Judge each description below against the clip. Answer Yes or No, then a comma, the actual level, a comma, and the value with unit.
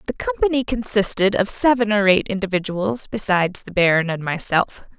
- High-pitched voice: Yes, high, 195 Hz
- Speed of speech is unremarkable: Yes, average, 155 wpm